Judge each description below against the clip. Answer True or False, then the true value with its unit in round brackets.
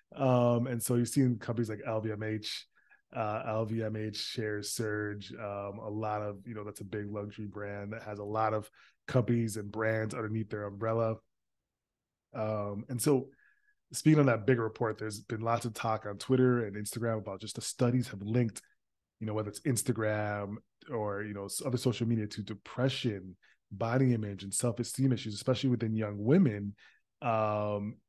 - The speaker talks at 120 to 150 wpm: False (170 wpm)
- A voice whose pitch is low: True (110 Hz)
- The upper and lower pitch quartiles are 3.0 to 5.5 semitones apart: False (2.5 semitones)